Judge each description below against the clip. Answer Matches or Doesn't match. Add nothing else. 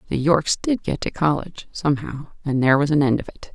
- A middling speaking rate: Doesn't match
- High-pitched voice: Doesn't match